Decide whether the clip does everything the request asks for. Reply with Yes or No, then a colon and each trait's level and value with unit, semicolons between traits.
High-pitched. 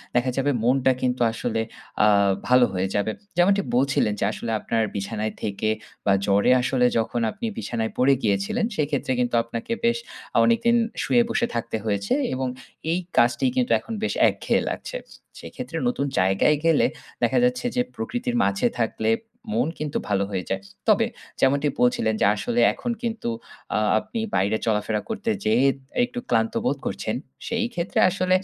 No: low, 125 Hz